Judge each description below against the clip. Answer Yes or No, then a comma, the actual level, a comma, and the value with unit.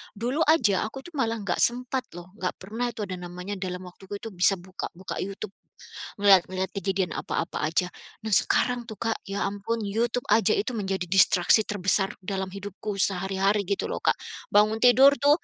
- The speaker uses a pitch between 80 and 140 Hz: No, high, 200 Hz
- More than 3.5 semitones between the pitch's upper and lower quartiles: No, average, 3.2 semitones